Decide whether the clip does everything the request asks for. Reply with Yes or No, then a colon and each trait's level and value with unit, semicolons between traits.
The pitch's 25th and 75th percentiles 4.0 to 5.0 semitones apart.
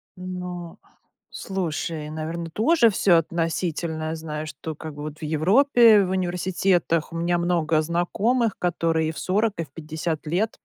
No: average, 2.8 semitones